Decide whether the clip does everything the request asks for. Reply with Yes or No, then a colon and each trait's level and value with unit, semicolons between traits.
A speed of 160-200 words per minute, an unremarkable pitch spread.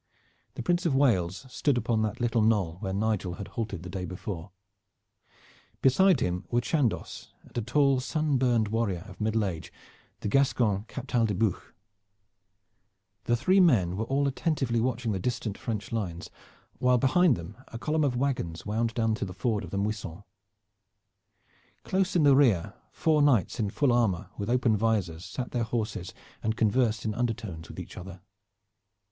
Yes: average, 170 wpm; average, 4.7 semitones